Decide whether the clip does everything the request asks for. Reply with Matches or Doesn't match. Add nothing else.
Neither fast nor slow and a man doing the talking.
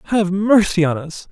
Matches